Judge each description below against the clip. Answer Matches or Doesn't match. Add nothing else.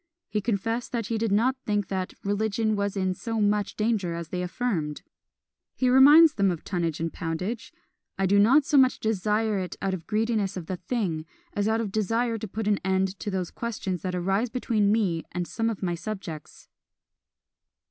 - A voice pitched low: Doesn't match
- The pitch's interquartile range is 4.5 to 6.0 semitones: Doesn't match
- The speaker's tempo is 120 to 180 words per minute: Doesn't match